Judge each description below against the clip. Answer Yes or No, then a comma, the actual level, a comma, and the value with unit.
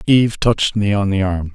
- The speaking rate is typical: No, fast, 235 wpm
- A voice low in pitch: Yes, low, 100 Hz